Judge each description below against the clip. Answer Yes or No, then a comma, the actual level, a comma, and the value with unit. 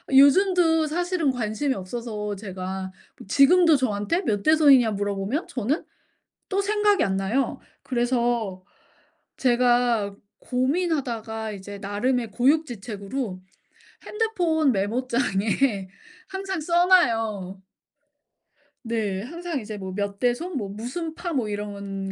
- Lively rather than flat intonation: Yes, wide, 7.4 semitones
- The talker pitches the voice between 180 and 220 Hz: No, high, 240 Hz